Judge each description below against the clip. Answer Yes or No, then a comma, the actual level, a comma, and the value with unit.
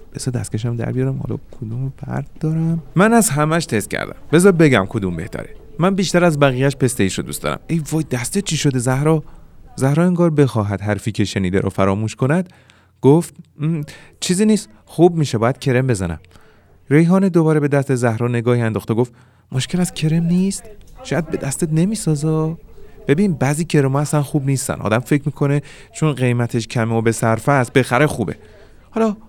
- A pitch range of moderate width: No, wide, 5.8 semitones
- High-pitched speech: No, medium, 140 Hz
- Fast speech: Yes, fast, 170 wpm